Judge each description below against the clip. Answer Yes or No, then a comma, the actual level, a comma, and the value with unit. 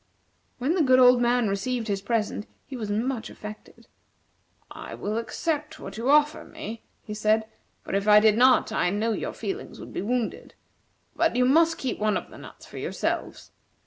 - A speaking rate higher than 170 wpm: Yes, average, 185 wpm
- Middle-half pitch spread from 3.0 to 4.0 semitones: Yes, average, 3.6 semitones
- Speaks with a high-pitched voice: Yes, high, 235 Hz